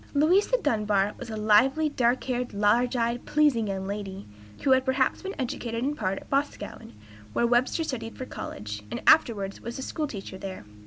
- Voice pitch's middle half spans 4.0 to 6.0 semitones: Yes, average, 4.6 semitones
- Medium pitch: No, high, 235 Hz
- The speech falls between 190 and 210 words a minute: No, average, 180 wpm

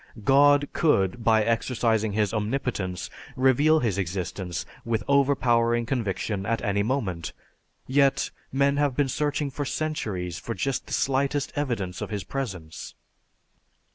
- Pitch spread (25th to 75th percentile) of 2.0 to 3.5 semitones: No, wide, 5.4 semitones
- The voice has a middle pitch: No, low, 120 Hz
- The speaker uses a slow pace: Yes, slow, 130 wpm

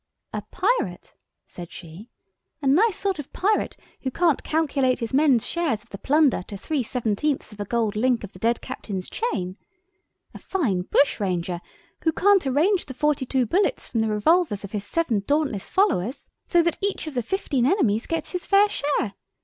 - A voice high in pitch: Yes, very high, 265 Hz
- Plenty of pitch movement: Yes, wide, 7.8 semitones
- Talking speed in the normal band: Yes, average, 180 wpm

